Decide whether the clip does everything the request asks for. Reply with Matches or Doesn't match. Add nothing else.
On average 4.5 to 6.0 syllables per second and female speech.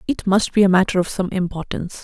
Doesn't match